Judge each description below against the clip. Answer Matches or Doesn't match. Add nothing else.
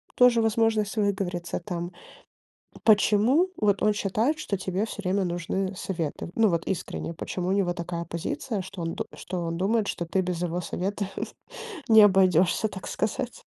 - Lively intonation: Doesn't match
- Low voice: Doesn't match